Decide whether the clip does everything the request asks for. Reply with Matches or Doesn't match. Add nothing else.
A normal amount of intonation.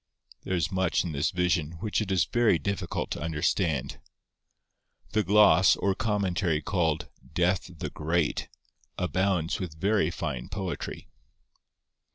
Matches